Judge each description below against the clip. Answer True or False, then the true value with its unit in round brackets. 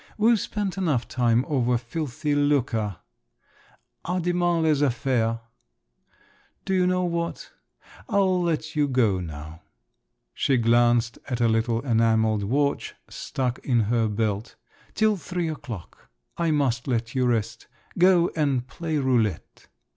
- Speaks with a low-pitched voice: True (130 Hz)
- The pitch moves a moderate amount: False (6.2 semitones)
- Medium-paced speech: False (130 wpm)